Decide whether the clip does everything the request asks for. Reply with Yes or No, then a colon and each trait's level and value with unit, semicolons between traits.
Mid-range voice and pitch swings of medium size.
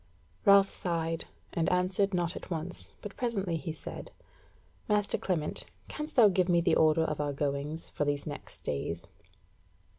Yes: medium, 170 Hz; average, 4.3 semitones